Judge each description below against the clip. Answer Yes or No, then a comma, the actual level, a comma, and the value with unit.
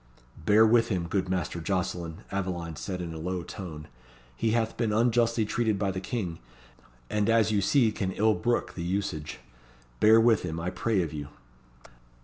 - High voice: No, very low, 95 Hz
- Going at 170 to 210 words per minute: Yes, average, 175 wpm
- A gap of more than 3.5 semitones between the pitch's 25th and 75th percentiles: Yes, average, 4.4 semitones